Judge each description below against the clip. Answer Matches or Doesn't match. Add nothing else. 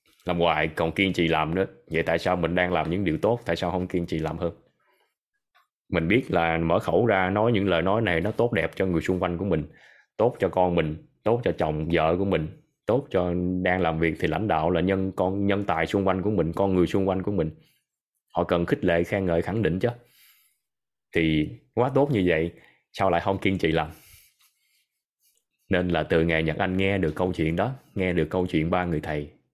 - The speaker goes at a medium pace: Matches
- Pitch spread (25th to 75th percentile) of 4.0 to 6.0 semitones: Doesn't match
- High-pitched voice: Doesn't match